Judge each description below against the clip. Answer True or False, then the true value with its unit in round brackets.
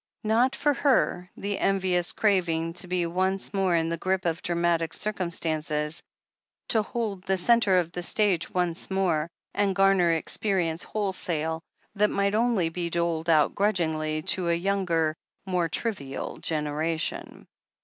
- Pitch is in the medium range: True (180 Hz)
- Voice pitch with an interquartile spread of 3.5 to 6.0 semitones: False (3.0 semitones)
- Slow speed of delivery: False (145 wpm)